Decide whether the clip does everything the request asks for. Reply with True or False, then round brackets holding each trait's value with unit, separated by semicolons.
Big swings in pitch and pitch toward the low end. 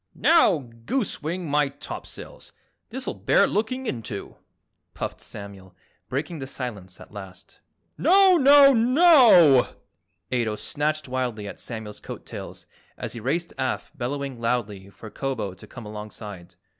True (8.9 semitones; 130 Hz)